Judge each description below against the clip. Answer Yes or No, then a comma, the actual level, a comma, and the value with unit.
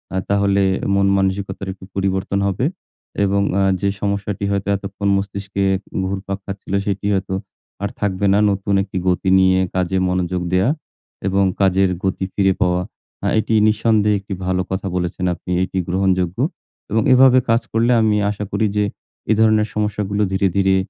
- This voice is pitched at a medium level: No, low, 100 Hz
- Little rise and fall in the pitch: Yes, narrow, 1.3 semitones